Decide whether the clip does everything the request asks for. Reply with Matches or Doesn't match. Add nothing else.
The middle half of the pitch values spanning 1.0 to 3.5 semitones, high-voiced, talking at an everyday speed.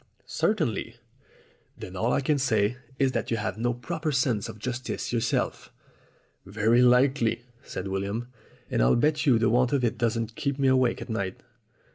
Doesn't match